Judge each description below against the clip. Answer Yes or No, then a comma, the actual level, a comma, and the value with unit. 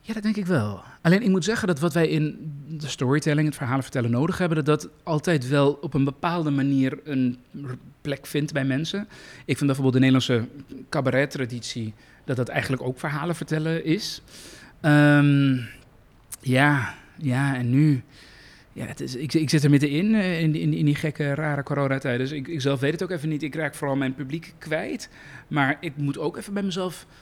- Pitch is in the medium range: Yes, medium, 145 Hz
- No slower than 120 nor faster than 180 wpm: No, average, 195 wpm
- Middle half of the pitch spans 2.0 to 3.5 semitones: Yes, average, 3.2 semitones